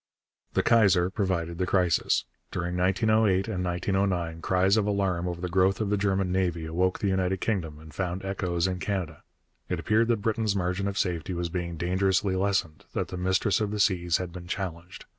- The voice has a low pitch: Yes, very low, 95 Hz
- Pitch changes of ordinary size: No, narrow, 2.0 semitones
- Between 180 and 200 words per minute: Yes, average, 190 wpm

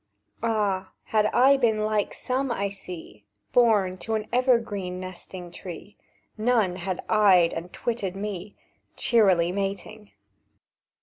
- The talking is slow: Yes, slow, 120 wpm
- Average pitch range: Yes, average, 3.3 semitones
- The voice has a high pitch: Yes, high, 200 Hz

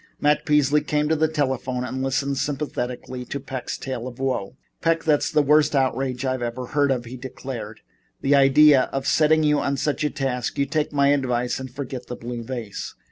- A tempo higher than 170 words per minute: Yes, average, 190 wpm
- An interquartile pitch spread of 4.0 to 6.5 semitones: No, average, 2.7 semitones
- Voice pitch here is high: No, low, 135 Hz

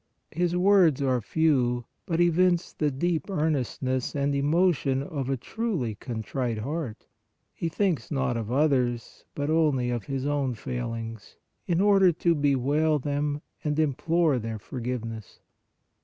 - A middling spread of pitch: Yes, average, 4.7 semitones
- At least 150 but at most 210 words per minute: No, slow, 135 wpm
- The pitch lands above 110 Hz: Yes, medium, 140 Hz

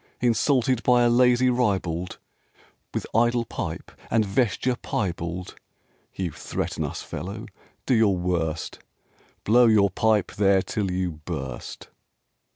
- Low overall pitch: Yes, low, 105 Hz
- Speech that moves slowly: Yes, slow, 120 wpm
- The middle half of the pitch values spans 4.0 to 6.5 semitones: Yes, average, 4.9 semitones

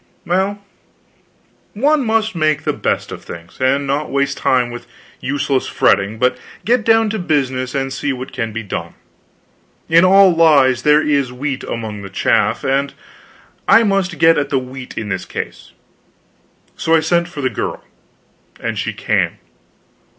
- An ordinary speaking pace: Yes, average, 160 wpm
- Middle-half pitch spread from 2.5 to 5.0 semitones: No, wide, 5.5 semitones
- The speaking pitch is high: No, medium, 140 Hz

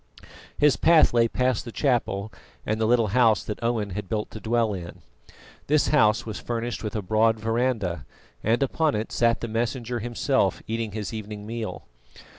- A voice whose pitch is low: Yes, low, 115 Hz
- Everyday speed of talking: Yes, average, 175 wpm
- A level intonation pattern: Yes, narrow, 2.2 semitones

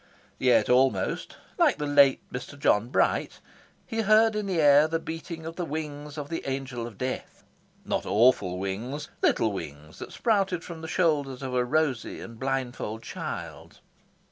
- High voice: No, medium, 140 Hz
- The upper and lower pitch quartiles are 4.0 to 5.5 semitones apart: Yes, average, 4.8 semitones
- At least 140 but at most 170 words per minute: Yes, average, 165 wpm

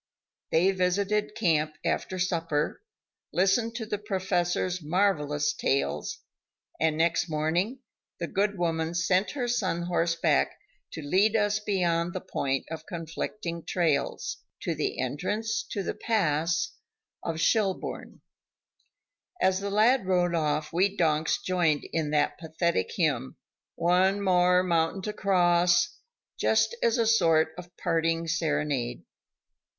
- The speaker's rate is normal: No, slow, 125 wpm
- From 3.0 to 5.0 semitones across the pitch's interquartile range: Yes, average, 3.4 semitones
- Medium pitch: Yes, medium, 175 Hz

